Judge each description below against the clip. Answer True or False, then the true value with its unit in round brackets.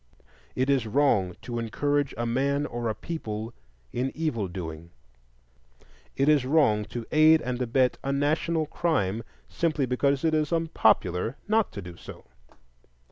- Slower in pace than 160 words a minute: True (145 wpm)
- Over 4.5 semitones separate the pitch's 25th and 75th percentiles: True (5.2 semitones)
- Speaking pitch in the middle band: False (130 Hz)